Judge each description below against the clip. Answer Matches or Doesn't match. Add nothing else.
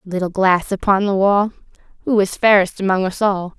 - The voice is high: Matches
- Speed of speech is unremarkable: Matches